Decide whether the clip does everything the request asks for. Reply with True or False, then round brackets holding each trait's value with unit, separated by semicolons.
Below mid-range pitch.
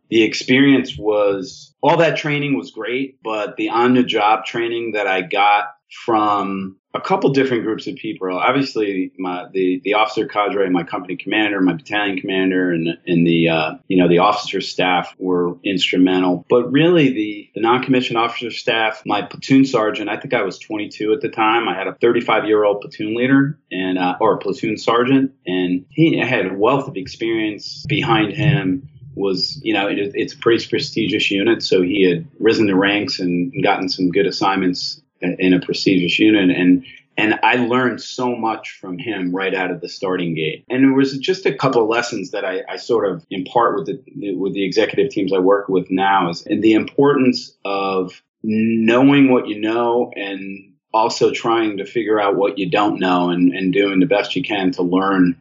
True (105 Hz)